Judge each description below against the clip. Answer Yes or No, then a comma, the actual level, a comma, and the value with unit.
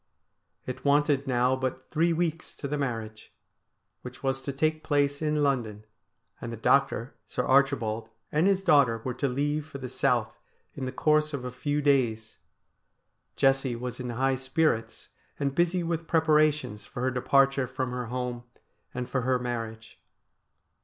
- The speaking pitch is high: No, low, 135 Hz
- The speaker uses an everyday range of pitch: Yes, average, 3.0 semitones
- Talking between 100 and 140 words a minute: No, average, 165 wpm